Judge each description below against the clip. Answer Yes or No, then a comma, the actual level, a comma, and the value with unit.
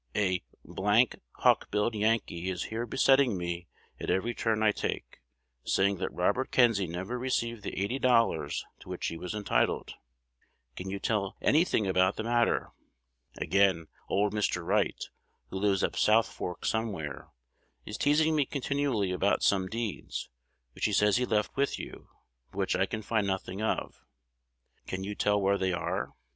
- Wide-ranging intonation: No, average, 3.5 semitones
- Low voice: Yes, low, 105 Hz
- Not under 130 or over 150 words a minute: No, average, 170 wpm